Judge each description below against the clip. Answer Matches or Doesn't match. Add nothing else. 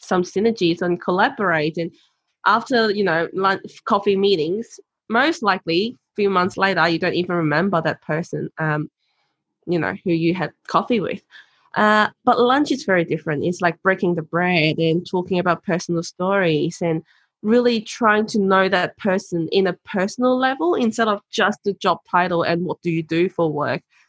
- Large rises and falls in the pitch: Doesn't match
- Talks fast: Doesn't match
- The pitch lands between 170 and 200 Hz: Matches